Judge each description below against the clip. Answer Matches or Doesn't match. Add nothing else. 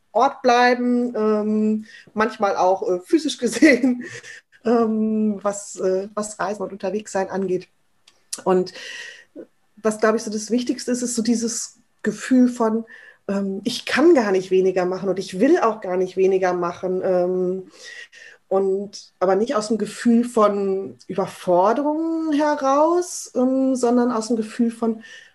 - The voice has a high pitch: Matches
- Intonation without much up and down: Doesn't match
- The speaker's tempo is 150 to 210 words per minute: Doesn't match